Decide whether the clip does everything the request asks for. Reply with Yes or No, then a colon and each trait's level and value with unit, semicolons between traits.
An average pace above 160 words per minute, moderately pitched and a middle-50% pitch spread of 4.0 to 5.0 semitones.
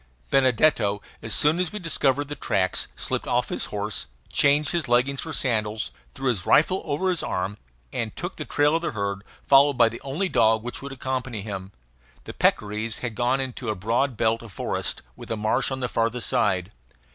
No: average, 195 wpm; low, 125 Hz; average, 4.6 semitones